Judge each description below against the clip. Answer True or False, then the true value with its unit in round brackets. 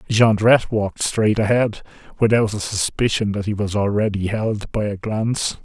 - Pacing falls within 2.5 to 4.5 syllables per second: False (5.1 syllables/s)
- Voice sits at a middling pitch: False (105 Hz)